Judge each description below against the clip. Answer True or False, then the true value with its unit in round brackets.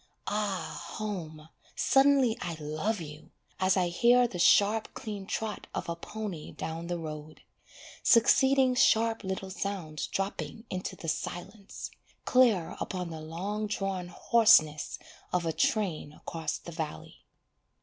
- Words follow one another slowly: True (130 wpm)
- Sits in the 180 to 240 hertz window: True (190 Hz)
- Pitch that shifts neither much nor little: True (5.0 semitones)